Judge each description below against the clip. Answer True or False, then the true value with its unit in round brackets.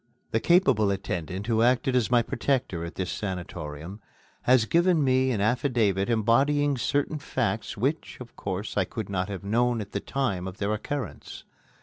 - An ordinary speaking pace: True (165 wpm)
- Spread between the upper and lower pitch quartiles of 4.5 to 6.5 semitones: True (4.8 semitones)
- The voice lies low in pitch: True (115 Hz)